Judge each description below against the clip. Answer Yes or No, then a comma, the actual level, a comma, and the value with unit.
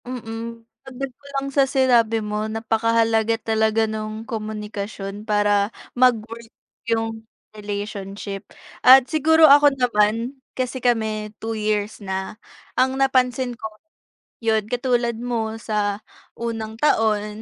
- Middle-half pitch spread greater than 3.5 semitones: No, narrow, 2.6 semitones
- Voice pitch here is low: No, high, 225 Hz